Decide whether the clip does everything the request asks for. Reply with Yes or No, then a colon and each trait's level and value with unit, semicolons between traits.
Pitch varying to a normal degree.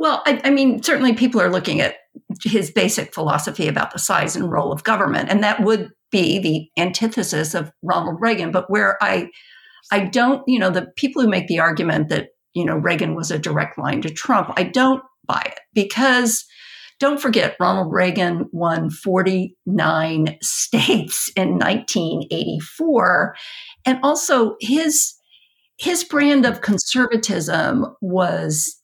No: wide, 6.3 semitones